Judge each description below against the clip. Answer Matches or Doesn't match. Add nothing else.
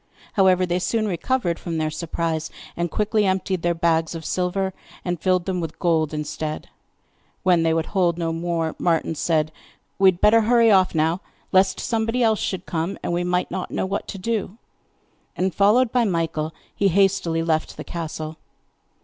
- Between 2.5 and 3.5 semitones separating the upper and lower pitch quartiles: Matches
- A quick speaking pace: Doesn't match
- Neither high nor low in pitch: Matches